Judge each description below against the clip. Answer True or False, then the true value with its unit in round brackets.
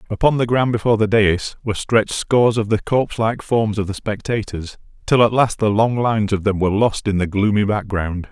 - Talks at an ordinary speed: False (215 wpm)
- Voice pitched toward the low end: True (105 Hz)